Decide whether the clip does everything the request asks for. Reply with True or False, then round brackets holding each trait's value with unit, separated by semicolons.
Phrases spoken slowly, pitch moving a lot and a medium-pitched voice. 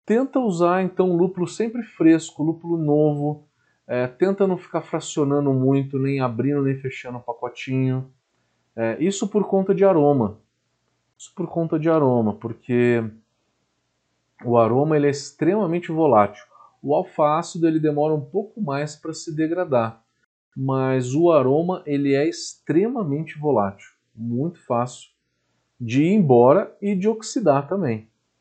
False (135 wpm; 5.9 semitones; 145 Hz)